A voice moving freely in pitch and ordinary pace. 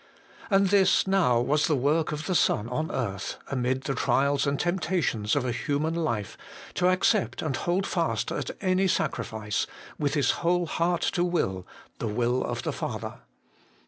Yes: wide, 6.2 semitones; average, 170 wpm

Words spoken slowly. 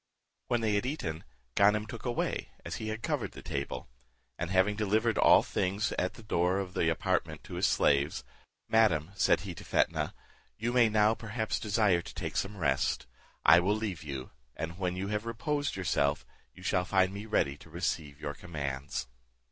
No: average, 185 wpm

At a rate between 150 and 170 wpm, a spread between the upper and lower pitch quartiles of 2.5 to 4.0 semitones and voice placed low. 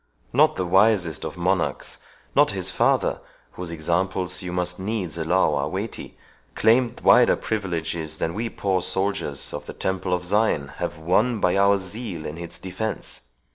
Yes: average, 160 wpm; average, 3.2 semitones; very low, 90 Hz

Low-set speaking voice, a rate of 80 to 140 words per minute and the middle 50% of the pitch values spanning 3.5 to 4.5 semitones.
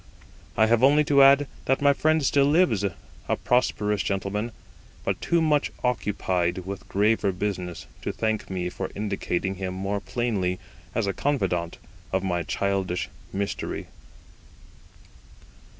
No: low, 100 Hz; slow, 135 wpm; average, 5.2 semitones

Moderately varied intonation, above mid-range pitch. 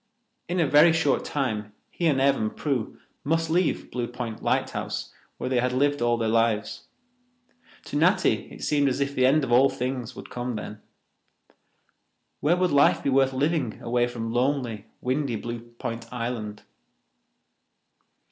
No: average, 3.5 semitones; low, 125 Hz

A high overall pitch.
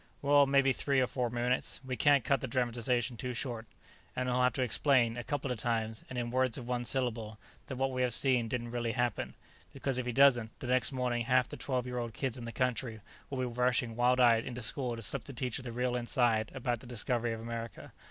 No: low, 125 Hz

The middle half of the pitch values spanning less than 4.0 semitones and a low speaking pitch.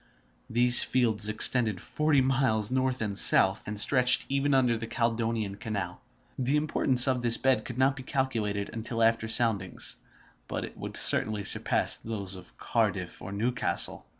Yes: average, 3.4 semitones; low, 115 Hz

